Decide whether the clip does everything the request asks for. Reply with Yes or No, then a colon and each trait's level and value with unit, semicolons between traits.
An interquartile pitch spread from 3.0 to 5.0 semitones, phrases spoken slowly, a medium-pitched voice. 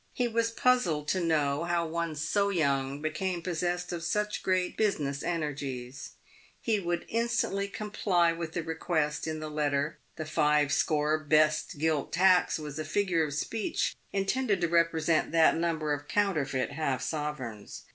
No: average, 3.6 semitones; average, 155 wpm; medium, 160 Hz